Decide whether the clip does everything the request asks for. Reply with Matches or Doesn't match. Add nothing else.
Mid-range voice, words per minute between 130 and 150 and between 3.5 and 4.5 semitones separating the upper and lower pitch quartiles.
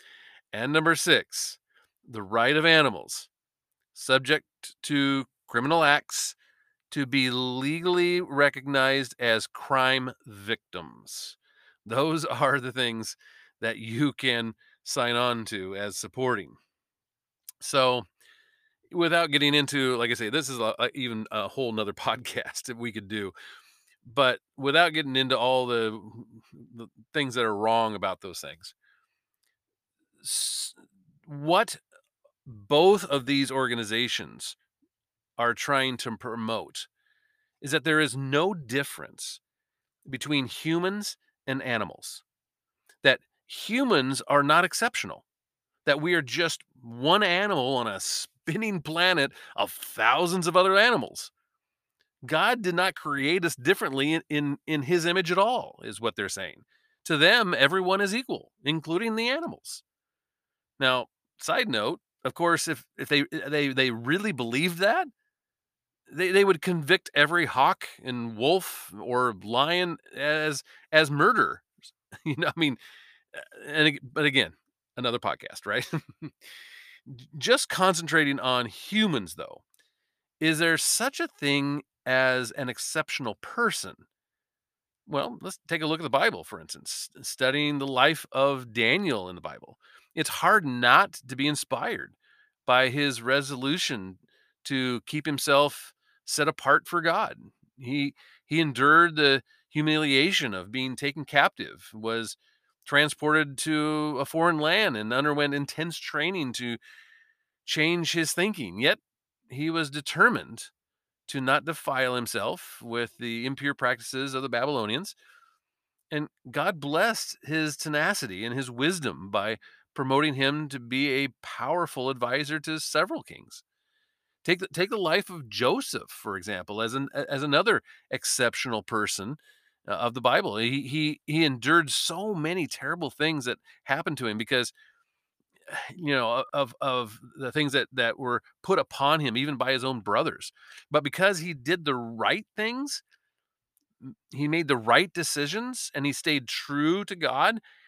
Doesn't match